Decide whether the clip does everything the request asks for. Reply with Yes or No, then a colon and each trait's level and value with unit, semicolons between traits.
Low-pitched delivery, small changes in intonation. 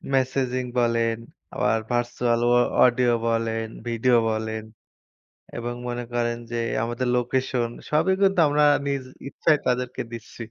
Yes: low, 120 Hz; narrow, 1.7 semitones